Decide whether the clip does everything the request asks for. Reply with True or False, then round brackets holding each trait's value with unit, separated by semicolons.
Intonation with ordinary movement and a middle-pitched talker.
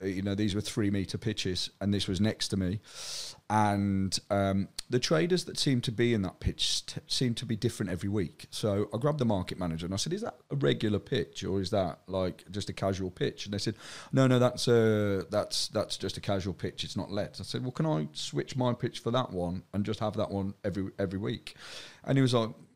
False (3.6 semitones; 105 Hz)